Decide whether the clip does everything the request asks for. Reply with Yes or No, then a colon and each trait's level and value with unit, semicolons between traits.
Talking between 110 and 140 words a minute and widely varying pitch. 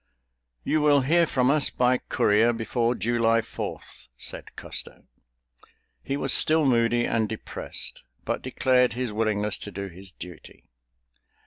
No: slow, 135 wpm; average, 3.3 semitones